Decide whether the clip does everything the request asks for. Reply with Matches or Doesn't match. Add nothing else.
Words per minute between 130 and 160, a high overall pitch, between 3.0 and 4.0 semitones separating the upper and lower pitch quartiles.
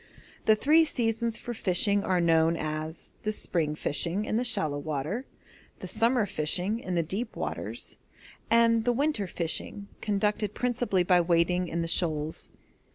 Doesn't match